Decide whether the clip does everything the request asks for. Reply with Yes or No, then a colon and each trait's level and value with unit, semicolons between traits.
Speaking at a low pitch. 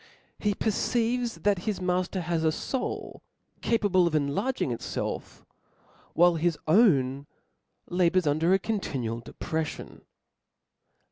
No: medium, 175 Hz